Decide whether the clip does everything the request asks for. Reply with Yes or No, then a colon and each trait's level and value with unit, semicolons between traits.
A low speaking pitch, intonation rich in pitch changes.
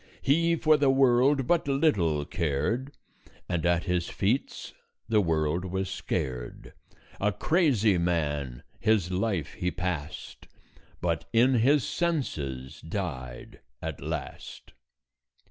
Yes: very low, 95 Hz; wide, 8.6 semitones